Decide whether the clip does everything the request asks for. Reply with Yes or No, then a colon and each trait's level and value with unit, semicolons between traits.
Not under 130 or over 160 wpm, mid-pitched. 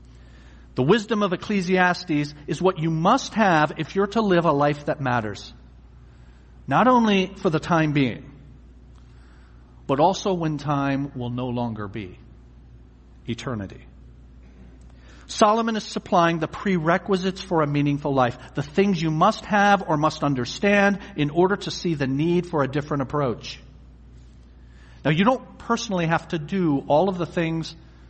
Yes: average, 150 wpm; medium, 150 Hz